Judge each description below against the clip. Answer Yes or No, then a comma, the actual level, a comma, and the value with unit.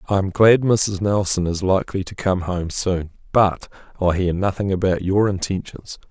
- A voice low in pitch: Yes, very low, 95 Hz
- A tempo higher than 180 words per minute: No, average, 175 wpm